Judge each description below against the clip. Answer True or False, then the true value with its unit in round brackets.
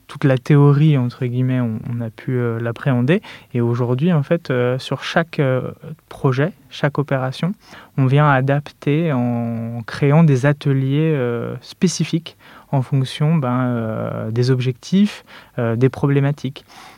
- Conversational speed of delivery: False (140 wpm)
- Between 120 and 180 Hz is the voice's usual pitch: True (135 Hz)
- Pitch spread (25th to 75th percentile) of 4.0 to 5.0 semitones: False (3.2 semitones)